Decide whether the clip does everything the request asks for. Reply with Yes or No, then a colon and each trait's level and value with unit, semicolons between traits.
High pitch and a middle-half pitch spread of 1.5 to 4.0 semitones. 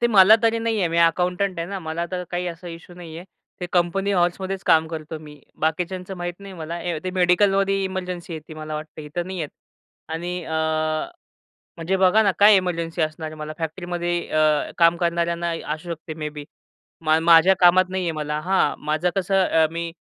No: medium, 175 Hz; narrow, 2.6 semitones